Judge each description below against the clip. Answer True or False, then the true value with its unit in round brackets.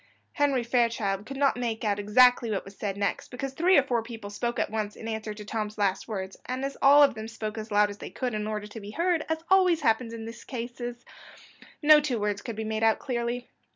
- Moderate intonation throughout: True (3.3 semitones)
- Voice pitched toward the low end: False (230 Hz)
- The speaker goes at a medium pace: False (240 wpm)